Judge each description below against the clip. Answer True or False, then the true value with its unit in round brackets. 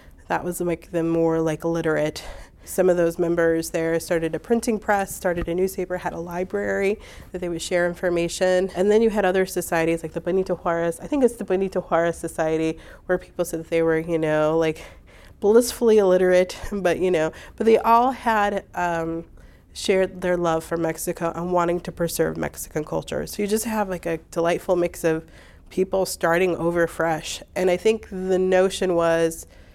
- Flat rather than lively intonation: True (2.2 semitones)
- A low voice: False (175 Hz)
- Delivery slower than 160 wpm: False (190 wpm)